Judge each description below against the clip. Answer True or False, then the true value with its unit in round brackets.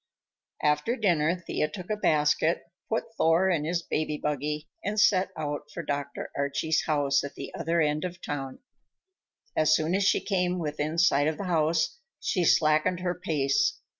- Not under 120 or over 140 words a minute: False (165 wpm)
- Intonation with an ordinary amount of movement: True (3.3 semitones)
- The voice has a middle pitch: True (155 Hz)